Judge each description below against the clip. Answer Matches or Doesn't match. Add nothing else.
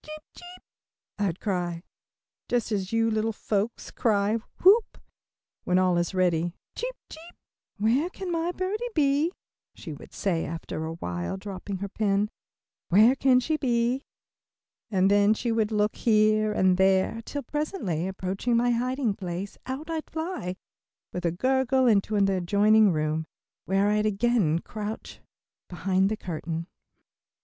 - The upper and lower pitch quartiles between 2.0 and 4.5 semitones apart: Doesn't match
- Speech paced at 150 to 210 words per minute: Doesn't match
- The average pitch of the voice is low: Doesn't match